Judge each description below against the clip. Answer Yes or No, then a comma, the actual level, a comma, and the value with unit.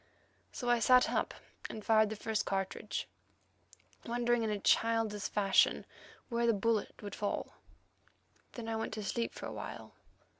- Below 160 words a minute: Yes, average, 150 wpm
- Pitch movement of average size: No, narrow, 2.1 semitones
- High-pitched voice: Yes, high, 225 Hz